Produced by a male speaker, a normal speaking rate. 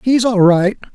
Yes: male; average, 190 wpm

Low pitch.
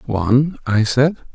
Yes: low, 130 Hz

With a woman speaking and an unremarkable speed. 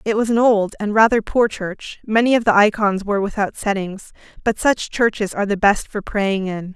No: female; fast, 215 wpm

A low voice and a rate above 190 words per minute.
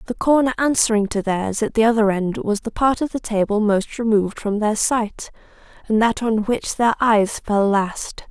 No: high, 220 Hz; average, 200 wpm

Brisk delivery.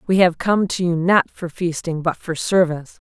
Yes: fast, 215 wpm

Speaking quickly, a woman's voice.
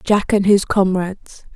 No: average, 155 wpm; female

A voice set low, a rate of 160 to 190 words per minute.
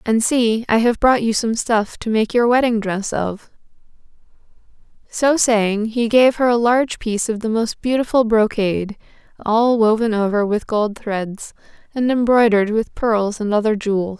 No: high, 225 Hz; average, 170 wpm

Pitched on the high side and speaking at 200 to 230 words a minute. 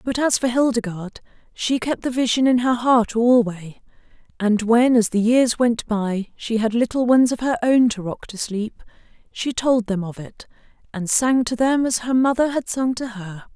Yes: high, 235 Hz; fast, 205 wpm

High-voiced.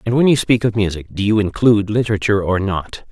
No: low, 105 Hz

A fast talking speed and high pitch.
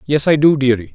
No: fast, 255 wpm; medium, 140 Hz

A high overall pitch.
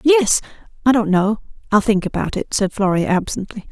Yes: high, 215 Hz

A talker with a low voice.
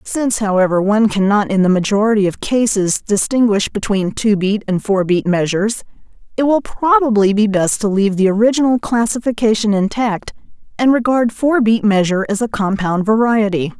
No: high, 215 Hz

